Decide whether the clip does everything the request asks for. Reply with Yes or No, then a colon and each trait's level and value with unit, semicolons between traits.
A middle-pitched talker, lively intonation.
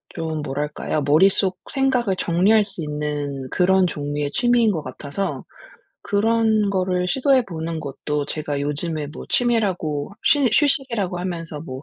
Yes: medium, 175 Hz; wide, 6.2 semitones